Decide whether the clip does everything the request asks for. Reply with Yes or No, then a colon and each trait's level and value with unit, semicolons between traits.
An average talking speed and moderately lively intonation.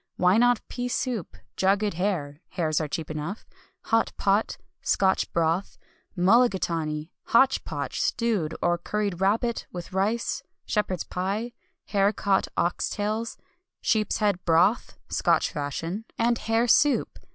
No: slow, 125 wpm; average, 4.6 semitones